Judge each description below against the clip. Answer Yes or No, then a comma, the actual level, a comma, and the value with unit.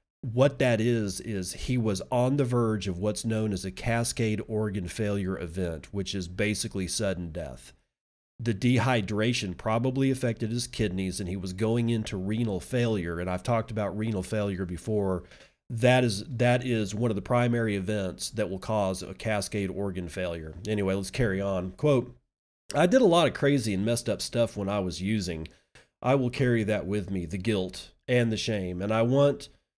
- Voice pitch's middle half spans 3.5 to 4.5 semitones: Yes, average, 3.8 semitones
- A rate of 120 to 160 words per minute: No, average, 185 wpm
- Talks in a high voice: No, low, 105 Hz